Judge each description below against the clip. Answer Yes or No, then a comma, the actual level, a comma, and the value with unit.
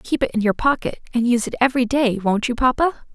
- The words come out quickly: Yes, fast, 250 wpm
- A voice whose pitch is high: Yes, very high, 250 Hz